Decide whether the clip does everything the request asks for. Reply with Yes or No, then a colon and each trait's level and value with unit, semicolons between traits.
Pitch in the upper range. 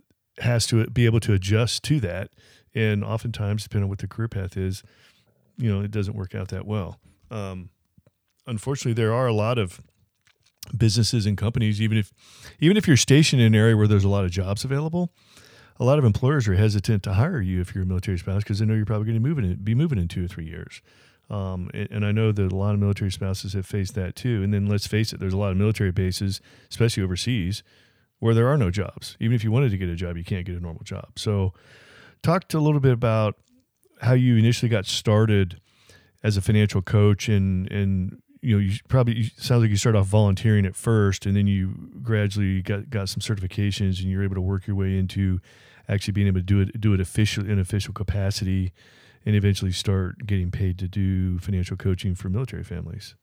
No: low, 105 Hz